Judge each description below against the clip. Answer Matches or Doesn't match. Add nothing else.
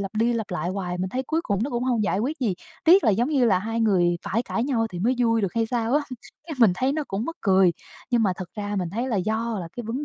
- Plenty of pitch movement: Doesn't match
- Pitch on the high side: Matches